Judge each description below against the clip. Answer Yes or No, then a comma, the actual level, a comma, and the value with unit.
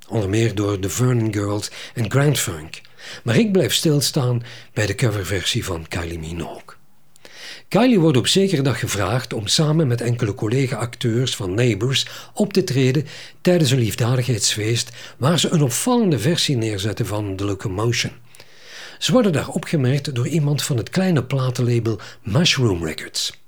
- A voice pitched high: No, low, 125 Hz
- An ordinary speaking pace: Yes, average, 150 wpm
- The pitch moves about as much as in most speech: Yes, average, 4.8 semitones